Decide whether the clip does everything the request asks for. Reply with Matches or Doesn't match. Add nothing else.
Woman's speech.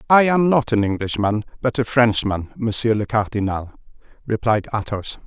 Doesn't match